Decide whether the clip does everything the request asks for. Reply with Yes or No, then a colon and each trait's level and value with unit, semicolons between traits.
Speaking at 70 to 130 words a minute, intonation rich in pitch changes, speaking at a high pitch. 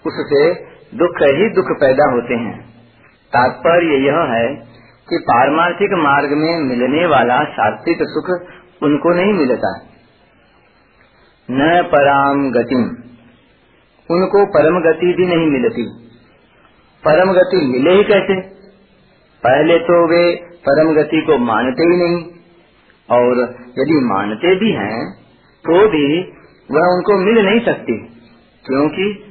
No: average, 115 wpm; wide, 5.8 semitones; medium, 165 Hz